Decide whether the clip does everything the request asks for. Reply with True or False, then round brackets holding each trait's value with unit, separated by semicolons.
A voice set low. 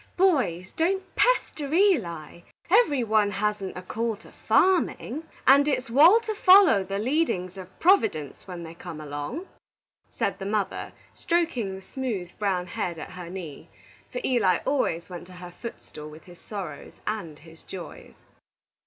False (205 Hz)